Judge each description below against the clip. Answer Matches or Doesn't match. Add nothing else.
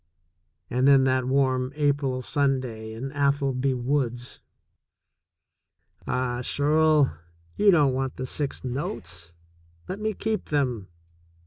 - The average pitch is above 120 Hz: Matches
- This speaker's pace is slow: Matches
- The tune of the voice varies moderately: Doesn't match